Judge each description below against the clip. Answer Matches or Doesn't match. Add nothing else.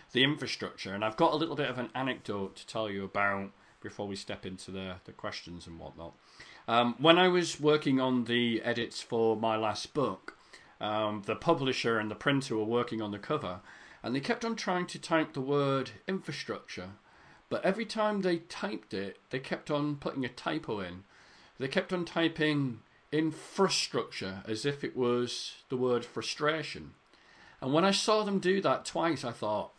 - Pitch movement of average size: Doesn't match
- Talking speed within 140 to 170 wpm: Doesn't match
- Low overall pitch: Matches